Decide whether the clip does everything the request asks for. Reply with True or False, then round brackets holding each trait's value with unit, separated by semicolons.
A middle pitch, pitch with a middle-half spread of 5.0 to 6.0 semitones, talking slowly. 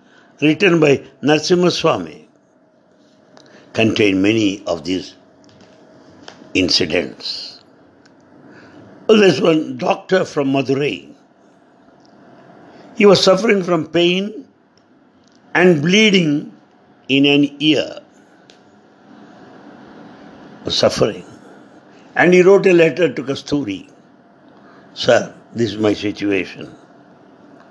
True (155 Hz; 5.6 semitones; 90 wpm)